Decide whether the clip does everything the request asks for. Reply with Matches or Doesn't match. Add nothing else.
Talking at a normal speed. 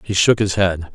Doesn't match